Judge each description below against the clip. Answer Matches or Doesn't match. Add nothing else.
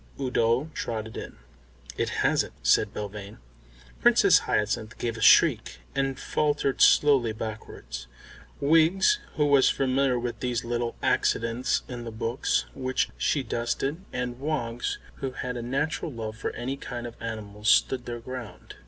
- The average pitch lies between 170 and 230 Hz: Doesn't match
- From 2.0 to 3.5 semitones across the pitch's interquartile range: Matches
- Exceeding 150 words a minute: Doesn't match